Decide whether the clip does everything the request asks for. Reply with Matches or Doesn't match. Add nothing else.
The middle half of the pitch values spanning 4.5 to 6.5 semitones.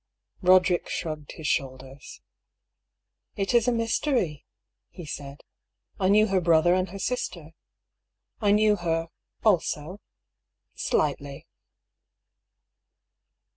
Matches